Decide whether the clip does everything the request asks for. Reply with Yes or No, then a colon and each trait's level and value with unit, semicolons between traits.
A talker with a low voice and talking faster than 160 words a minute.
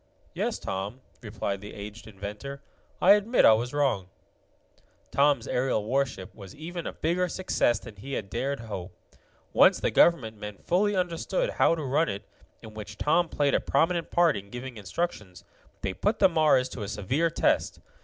Yes: low, 130 Hz; average, 175 wpm